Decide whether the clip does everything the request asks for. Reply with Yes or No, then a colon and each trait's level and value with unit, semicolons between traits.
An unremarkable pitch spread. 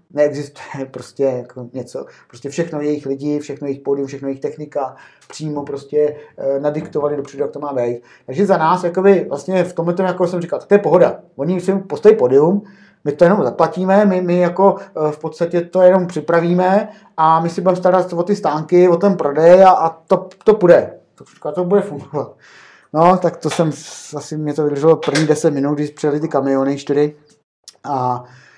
Yes: average, 4.0 semitones